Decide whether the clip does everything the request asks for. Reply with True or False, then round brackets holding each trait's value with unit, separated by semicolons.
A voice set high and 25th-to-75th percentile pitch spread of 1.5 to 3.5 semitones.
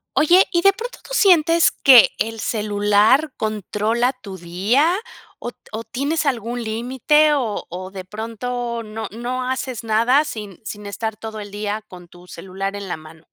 False (225 Hz; 4.2 semitones)